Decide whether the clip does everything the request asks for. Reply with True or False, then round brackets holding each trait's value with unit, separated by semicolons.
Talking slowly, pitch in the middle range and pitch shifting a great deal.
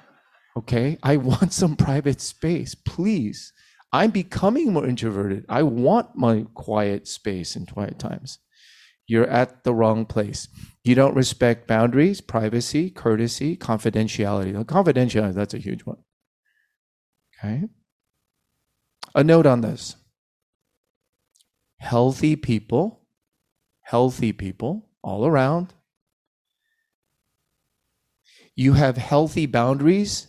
False (100 wpm; 125 Hz; 5.7 semitones)